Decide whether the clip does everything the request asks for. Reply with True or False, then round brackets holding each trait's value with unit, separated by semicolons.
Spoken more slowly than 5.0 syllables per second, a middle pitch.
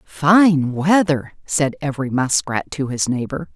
True (4.0 syllables/s; 145 Hz)